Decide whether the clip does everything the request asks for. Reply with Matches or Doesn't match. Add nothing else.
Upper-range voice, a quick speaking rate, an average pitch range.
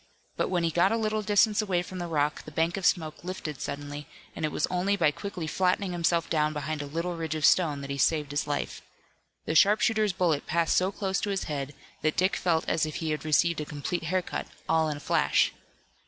Doesn't match